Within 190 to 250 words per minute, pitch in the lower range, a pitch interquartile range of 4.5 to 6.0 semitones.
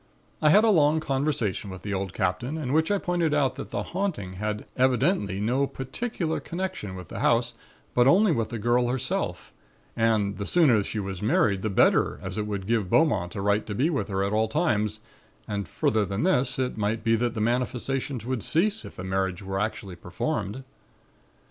Yes: average, 200 wpm; low, 115 Hz; wide, 5.6 semitones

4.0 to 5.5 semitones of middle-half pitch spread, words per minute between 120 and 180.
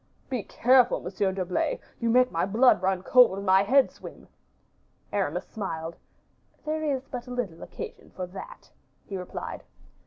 Yes: average, 5.2 semitones; average, 150 wpm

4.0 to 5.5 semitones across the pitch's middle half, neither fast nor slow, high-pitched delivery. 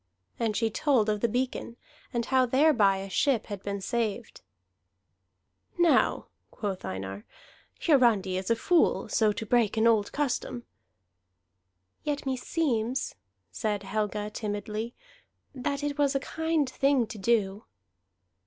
No: average, 4.4 semitones; slow, 130 wpm; high, 230 Hz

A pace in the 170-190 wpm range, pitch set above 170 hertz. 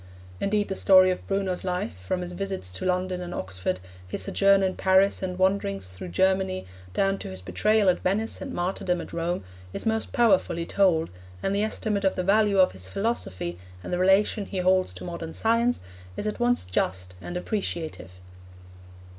Yes: average, 180 wpm; medium, 185 Hz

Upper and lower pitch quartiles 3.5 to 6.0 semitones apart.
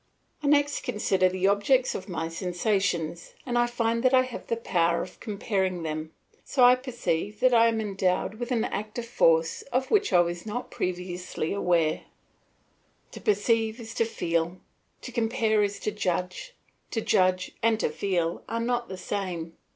Yes: average, 4.6 semitones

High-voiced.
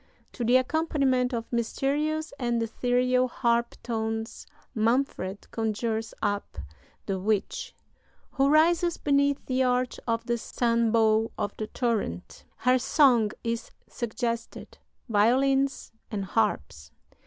Yes: high, 235 Hz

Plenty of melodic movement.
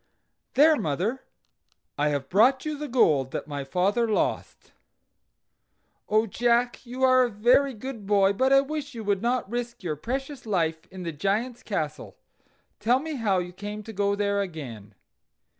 Yes: wide, 5.7 semitones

